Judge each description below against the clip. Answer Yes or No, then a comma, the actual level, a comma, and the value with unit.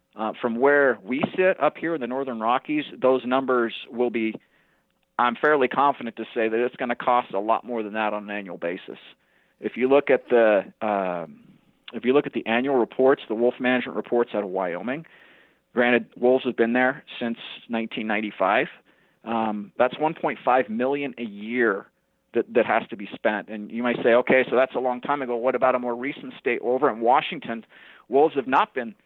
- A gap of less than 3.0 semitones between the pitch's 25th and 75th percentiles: Yes, narrow, 2.4 semitones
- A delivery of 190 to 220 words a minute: Yes, average, 200 wpm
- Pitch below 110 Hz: No, low, 120 Hz